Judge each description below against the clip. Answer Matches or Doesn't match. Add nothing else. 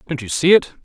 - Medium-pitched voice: Matches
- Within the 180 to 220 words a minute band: Doesn't match